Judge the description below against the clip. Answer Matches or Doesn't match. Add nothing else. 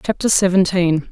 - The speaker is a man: Doesn't match